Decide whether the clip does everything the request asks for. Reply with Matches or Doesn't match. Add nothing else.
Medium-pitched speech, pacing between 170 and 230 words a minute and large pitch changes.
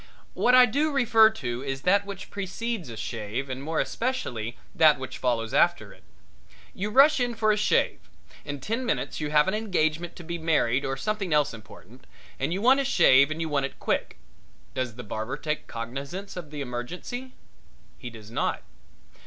Matches